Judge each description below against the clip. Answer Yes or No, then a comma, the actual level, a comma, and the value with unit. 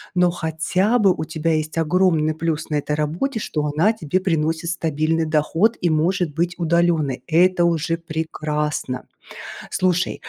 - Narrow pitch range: Yes, narrow, 2.3 semitones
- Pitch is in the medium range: Yes, medium, 165 Hz